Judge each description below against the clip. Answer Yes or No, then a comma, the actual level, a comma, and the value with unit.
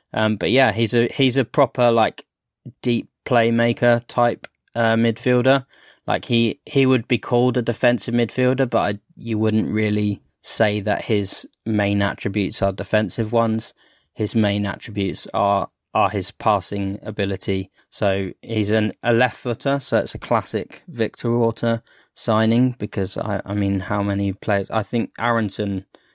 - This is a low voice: Yes, low, 110 Hz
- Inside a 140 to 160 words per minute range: Yes, average, 155 wpm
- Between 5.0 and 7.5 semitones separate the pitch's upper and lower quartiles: No, average, 2.8 semitones